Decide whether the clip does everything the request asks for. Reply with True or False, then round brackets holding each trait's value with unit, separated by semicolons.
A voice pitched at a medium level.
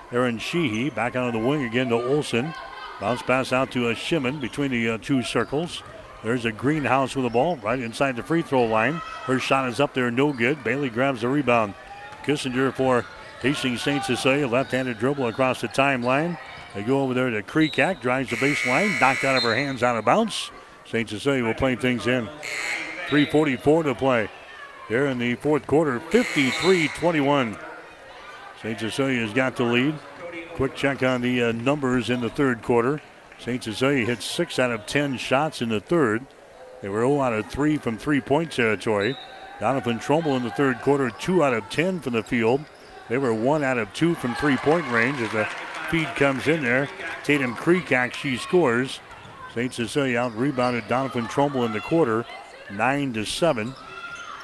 False (130 Hz)